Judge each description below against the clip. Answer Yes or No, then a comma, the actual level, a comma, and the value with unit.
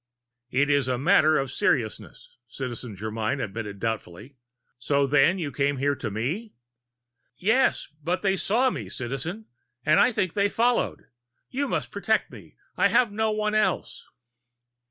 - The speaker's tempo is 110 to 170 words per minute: Yes, average, 150 wpm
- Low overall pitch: No, medium, 145 Hz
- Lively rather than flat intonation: Yes, wide, 8.9 semitones